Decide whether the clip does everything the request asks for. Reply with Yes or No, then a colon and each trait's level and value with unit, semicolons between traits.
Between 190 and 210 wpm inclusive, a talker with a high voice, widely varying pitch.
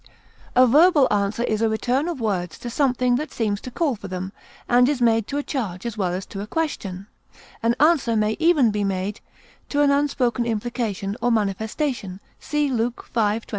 No: average, 195 wpm; high, 235 Hz; average, 4.8 semitones